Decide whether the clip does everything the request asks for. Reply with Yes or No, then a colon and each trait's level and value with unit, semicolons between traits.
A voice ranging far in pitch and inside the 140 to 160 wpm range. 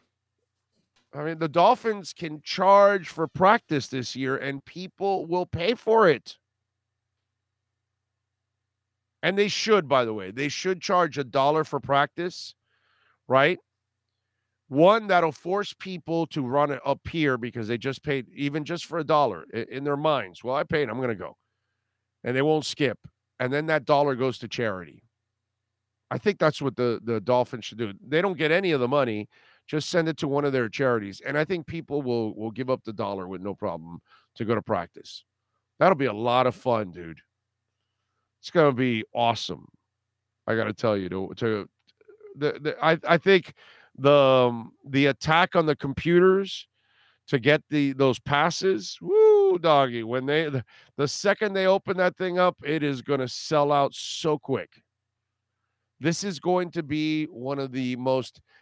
No: wide, 6.4 semitones; average, 175 wpm